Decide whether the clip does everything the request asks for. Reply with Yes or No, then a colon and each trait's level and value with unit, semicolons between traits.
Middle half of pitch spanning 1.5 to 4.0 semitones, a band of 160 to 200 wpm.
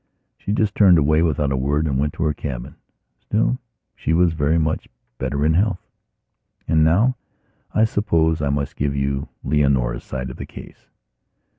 Yes: average, 3.1 semitones; average, 170 wpm